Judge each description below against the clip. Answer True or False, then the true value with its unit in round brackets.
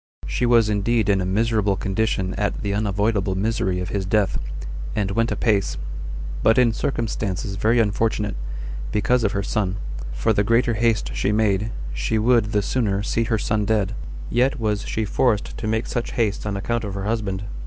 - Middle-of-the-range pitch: False (105 Hz)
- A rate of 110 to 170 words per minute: False (180 wpm)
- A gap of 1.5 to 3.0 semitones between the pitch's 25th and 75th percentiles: True (2.4 semitones)